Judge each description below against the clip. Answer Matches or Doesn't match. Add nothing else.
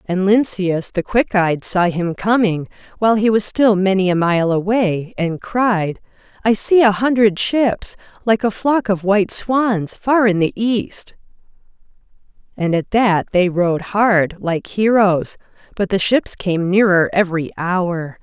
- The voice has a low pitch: Doesn't match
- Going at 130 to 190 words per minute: Matches